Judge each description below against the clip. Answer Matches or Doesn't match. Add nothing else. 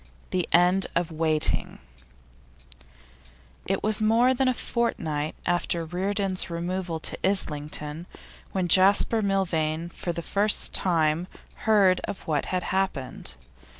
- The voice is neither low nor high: Matches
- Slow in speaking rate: Matches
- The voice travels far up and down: Doesn't match